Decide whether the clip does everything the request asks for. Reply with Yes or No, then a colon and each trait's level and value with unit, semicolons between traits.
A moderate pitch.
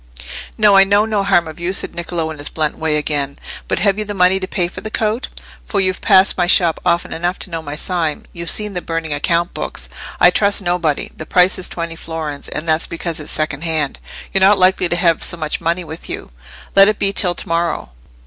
Yes: medium, 175 Hz